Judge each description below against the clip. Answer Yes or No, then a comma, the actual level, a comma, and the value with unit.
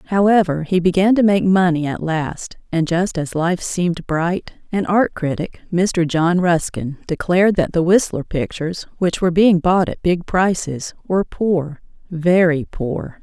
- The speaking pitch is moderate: Yes, medium, 175 Hz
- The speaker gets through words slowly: No, average, 160 wpm